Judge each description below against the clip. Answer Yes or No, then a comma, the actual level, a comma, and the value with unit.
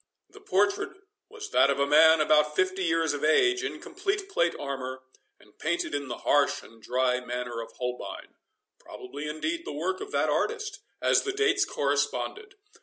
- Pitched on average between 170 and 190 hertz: No, medium, 160 Hz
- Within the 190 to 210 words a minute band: No, average, 170 wpm